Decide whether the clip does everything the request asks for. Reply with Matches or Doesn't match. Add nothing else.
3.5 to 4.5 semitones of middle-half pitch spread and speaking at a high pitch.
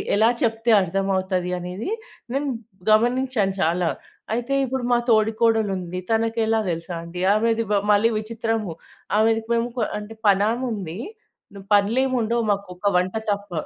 Doesn't match